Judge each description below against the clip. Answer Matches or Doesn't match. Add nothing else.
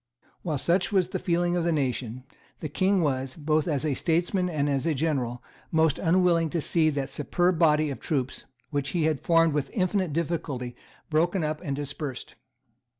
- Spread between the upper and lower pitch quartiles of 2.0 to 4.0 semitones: Matches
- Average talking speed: Matches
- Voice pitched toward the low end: Doesn't match